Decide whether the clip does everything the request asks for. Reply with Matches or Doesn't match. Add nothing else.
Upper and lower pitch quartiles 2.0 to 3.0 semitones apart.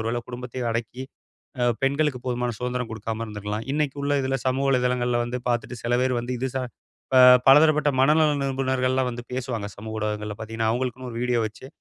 Matches